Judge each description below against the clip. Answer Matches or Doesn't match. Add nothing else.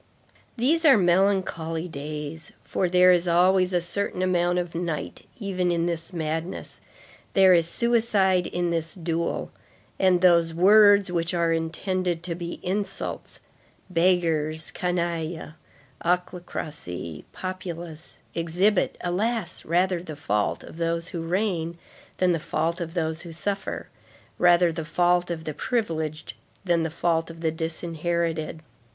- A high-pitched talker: Doesn't match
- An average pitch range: Doesn't match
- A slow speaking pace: Matches